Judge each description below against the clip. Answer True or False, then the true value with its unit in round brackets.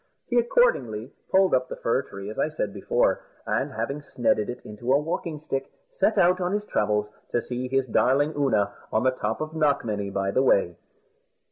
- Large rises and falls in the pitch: True (6.3 semitones)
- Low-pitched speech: True (130 Hz)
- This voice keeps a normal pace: True (195 wpm)